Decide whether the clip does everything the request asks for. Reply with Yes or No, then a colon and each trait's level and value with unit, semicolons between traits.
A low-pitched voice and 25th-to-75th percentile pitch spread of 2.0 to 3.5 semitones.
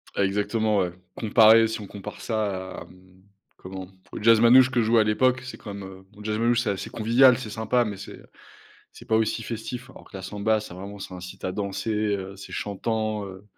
Yes: low, 105 Hz; narrow, 2.6 semitones